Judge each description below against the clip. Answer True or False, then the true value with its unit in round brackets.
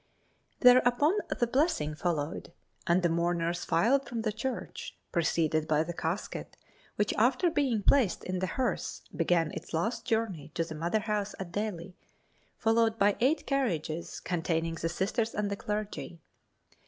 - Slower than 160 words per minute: True (150 wpm)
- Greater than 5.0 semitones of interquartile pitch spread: True (5.6 semitones)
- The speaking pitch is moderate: False (200 Hz)